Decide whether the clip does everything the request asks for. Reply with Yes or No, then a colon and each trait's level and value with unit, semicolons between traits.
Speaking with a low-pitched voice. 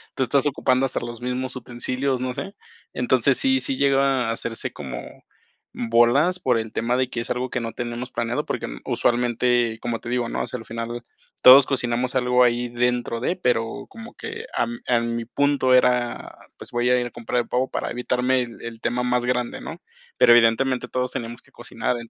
Yes: low, 125 Hz